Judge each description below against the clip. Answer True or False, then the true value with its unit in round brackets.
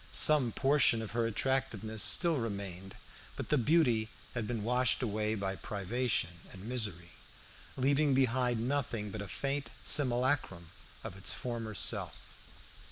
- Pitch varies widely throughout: False (4.4 semitones)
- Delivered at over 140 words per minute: False (135 wpm)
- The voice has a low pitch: True (115 Hz)